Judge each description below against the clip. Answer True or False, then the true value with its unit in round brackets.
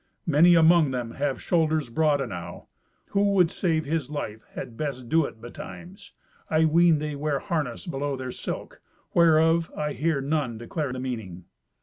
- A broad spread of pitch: False (4.2 semitones)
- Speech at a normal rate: True (160 wpm)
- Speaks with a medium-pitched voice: True (150 Hz)